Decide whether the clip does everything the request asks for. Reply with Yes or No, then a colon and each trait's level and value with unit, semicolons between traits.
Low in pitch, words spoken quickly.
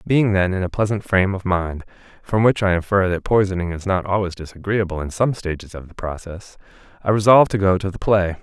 Yes: very low, 95 Hz; fast, 220 wpm